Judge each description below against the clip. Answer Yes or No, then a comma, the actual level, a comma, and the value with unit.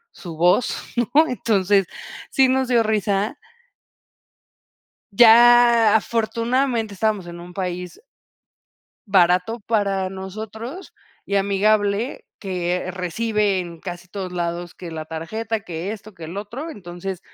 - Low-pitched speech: No, high, 200 Hz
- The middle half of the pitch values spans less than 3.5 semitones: No, average, 3.8 semitones